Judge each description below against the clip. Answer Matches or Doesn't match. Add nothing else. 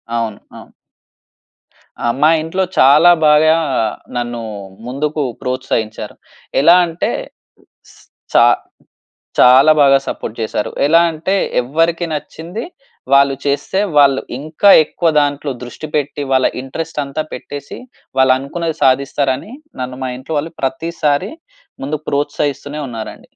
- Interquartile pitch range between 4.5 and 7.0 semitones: Doesn't match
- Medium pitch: Matches